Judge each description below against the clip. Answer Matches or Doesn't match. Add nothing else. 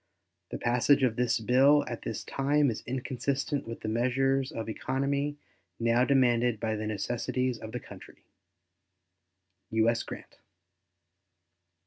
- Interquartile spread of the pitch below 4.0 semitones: Matches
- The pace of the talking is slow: Matches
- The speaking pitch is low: Matches